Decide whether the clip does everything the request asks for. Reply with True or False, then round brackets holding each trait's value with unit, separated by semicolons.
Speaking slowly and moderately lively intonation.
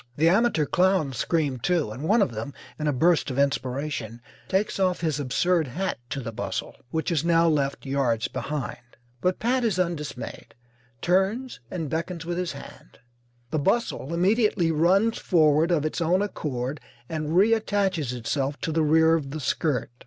False (165 wpm; 4.5 semitones)